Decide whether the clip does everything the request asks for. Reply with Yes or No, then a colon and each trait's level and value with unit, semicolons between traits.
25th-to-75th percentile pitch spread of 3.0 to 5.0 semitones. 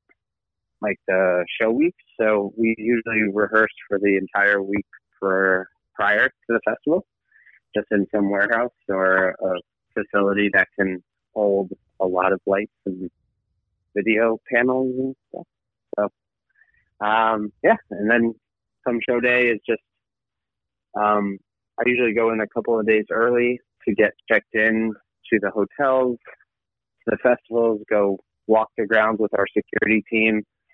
No: narrow, 2.5 semitones